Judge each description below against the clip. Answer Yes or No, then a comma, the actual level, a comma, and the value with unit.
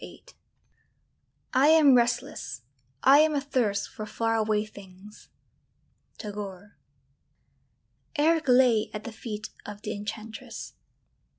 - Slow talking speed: Yes, slow, 105 wpm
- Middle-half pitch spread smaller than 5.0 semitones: Yes, average, 4.1 semitones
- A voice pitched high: Yes, high, 220 Hz